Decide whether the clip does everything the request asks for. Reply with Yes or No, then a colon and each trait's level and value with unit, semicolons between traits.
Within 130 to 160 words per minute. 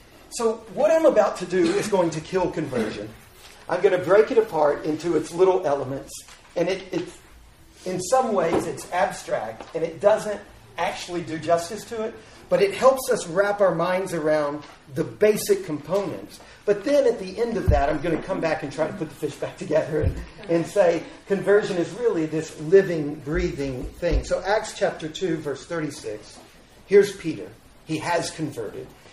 No: average, 185 wpm